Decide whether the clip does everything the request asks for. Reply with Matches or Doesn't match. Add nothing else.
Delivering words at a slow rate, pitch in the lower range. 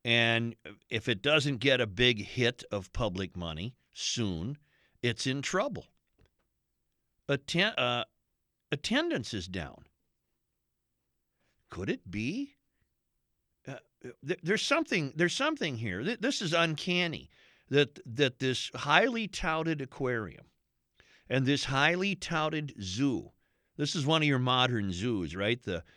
Matches